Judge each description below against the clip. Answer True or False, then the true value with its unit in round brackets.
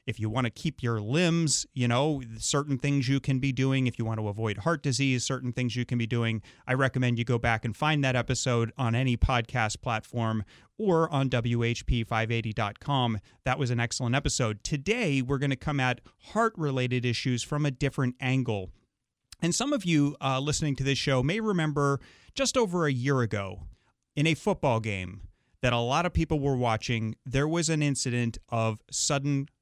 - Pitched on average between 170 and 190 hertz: False (130 Hz)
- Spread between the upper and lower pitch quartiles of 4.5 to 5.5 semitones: False (3.5 semitones)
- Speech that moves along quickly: False (195 wpm)